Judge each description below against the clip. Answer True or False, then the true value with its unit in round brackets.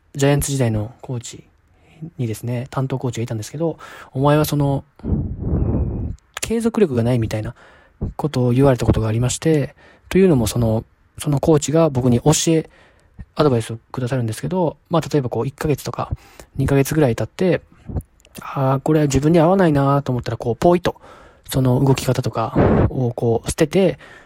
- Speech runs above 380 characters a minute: False (360 characters per minute)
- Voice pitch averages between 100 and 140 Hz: True (135 Hz)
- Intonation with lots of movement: False (4.7 semitones)